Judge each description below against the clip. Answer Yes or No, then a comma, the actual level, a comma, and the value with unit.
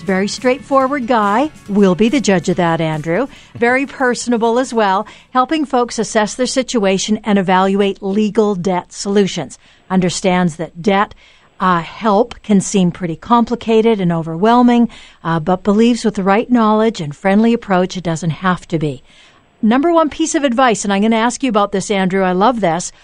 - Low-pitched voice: No, high, 205 Hz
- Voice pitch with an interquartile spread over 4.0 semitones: Yes, average, 4.4 semitones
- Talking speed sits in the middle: Yes, average, 175 wpm